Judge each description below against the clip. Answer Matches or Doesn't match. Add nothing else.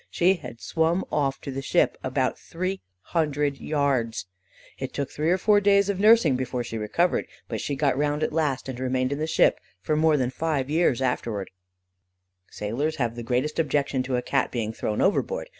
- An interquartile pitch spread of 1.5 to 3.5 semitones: Doesn't match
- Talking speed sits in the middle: Matches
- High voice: Doesn't match